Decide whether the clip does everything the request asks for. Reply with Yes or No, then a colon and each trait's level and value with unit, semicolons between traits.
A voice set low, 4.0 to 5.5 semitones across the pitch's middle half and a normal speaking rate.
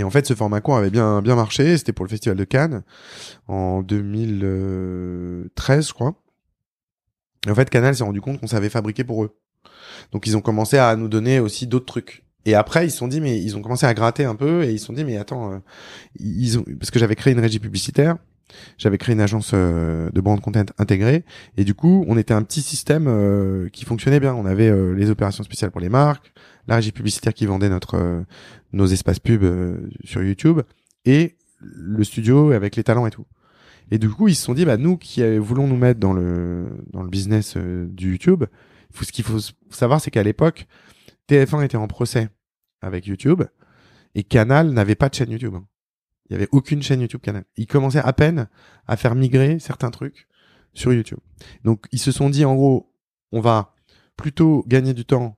Yes: low, 115 Hz; average, 4.6 semitones; average, 205 wpm